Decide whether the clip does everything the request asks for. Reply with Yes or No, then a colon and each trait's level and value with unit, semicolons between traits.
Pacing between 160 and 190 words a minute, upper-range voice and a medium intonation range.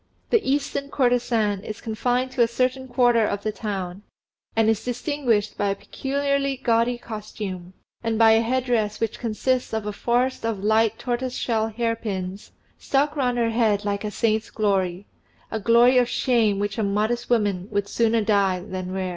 Yes: average, 170 wpm; high, 225 Hz; average, 3.1 semitones